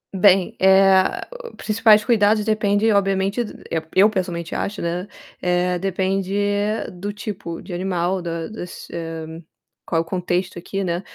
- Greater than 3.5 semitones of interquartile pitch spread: No, narrow, 2.5 semitones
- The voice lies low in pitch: No, high, 190 Hz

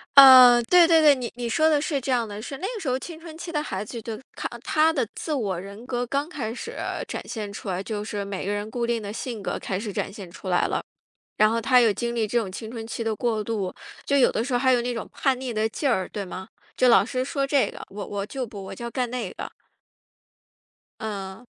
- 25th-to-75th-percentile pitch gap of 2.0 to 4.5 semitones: Yes, average, 4.1 semitones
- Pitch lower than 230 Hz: No, high, 235 Hz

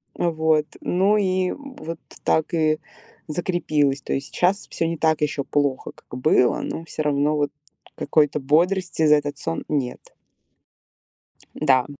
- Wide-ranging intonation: No, average, 2.9 semitones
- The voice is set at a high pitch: No, medium, 155 Hz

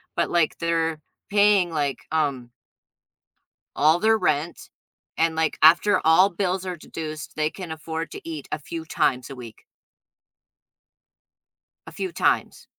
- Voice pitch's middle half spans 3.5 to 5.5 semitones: No, narrow, 2.5 semitones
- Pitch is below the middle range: No, medium, 160 Hz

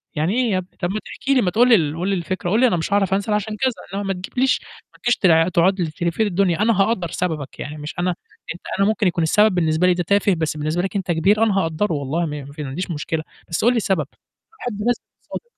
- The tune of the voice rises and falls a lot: No, average, 4.3 semitones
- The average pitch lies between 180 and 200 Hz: Yes, medium, 185 Hz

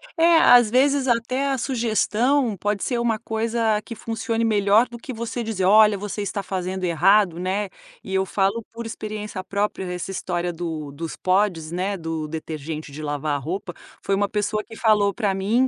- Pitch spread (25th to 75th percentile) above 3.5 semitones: Yes, average, 3.9 semitones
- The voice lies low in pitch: No, high, 205 Hz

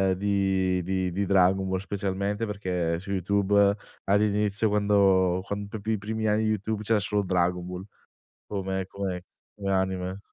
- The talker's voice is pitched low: Yes, low, 100 Hz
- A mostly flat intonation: Yes, narrow, 1.7 semitones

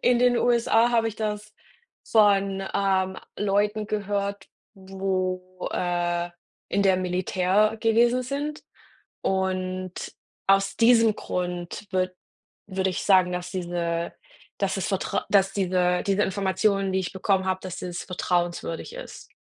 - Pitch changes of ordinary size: No, narrow, 2.2 semitones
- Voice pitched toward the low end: No, high, 190 Hz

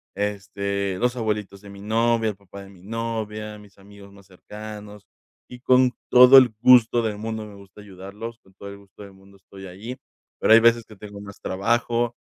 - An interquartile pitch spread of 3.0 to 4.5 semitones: No, narrow, 2.5 semitones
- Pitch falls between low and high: No, low, 105 Hz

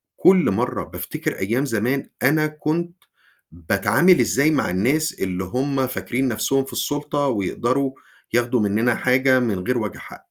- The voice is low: Yes, low, 130 Hz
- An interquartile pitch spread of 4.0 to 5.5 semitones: Yes, average, 4.7 semitones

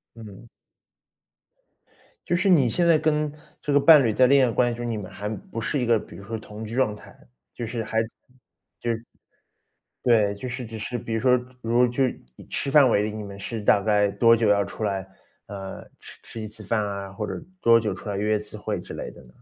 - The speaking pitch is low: Yes, low, 115 Hz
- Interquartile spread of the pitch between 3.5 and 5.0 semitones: No, average, 3.0 semitones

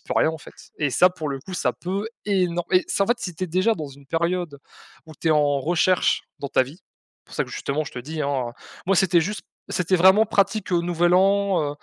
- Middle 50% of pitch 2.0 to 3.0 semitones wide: No, average, 3.8 semitones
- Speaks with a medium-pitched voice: Yes, medium, 175 Hz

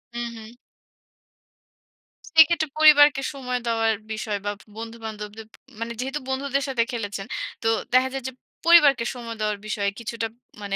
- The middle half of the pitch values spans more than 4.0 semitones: No, average, 3.7 semitones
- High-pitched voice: Yes, high, 235 Hz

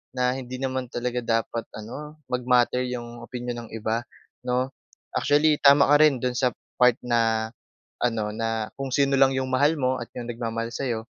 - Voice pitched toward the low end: Yes, low, 125 Hz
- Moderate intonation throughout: No, narrow, 2.2 semitones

